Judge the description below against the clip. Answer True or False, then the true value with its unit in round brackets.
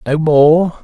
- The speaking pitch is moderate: True (155 Hz)